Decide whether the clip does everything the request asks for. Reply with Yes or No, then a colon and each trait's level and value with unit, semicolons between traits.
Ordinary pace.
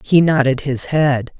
Yes: average, 175 wpm